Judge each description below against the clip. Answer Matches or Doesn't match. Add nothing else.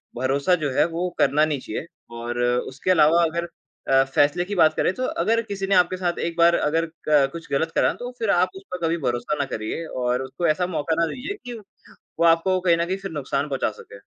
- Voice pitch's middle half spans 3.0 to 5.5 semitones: Matches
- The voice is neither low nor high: Matches